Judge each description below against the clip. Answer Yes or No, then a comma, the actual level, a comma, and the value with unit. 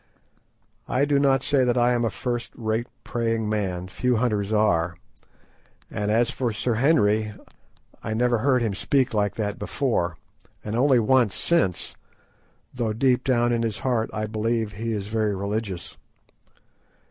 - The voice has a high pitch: No, low, 115 Hz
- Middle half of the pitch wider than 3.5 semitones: No, average, 2.7 semitones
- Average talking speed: Yes, average, 160 wpm